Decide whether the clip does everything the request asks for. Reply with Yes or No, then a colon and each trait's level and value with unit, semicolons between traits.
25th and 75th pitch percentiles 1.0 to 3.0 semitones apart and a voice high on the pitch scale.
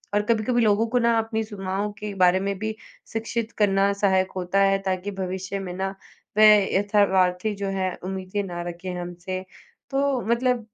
Yes: narrow, 2.6 semitones; high, 195 Hz